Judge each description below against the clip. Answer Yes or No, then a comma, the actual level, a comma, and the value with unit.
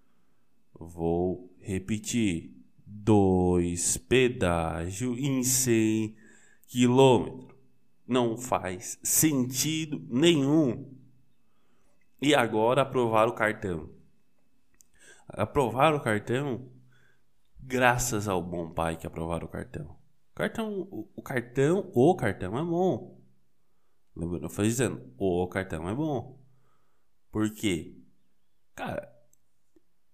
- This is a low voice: Yes, low, 110 Hz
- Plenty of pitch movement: Yes, wide, 6.3 semitones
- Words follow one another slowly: Yes, slow, 90 wpm